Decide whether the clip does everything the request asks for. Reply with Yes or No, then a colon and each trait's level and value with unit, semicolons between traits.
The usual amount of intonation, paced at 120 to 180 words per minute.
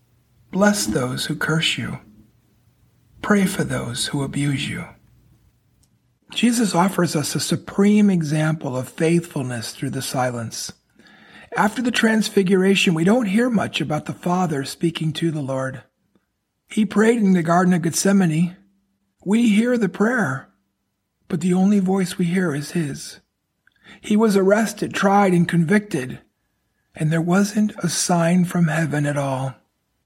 No: wide, 5.7 semitones; average, 140 wpm